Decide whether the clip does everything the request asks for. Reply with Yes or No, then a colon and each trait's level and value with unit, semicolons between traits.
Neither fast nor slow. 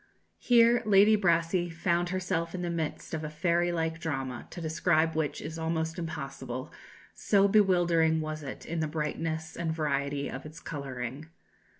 Yes: average, 160 wpm